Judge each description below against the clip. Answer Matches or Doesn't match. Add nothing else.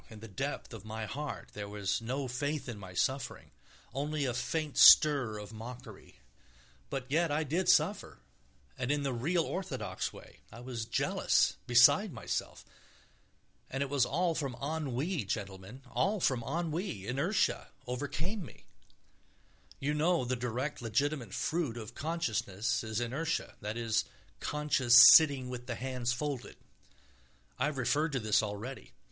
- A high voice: Doesn't match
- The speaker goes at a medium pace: Matches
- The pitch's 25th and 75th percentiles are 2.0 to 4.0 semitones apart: Doesn't match